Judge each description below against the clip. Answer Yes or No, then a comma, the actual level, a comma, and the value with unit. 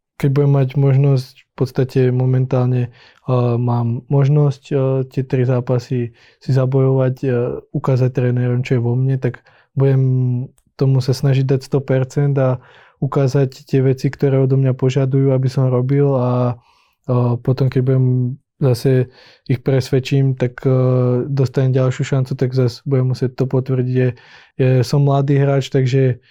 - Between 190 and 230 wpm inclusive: No, average, 150 wpm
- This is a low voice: Yes, low, 130 Hz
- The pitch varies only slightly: Yes, narrow, 1.4 semitones